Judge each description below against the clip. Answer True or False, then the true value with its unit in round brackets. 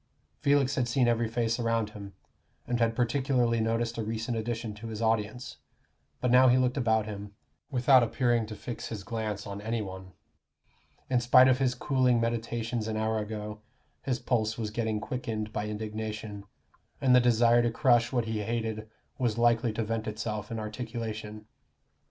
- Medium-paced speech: True (170 wpm)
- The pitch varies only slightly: True (2.0 semitones)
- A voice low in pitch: True (115 Hz)